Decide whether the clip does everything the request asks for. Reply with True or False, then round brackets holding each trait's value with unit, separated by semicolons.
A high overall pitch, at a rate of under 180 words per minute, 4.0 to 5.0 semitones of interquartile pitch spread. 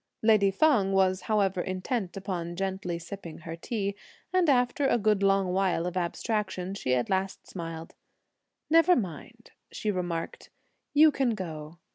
False (195 Hz; 145 wpm; 3.6 semitones)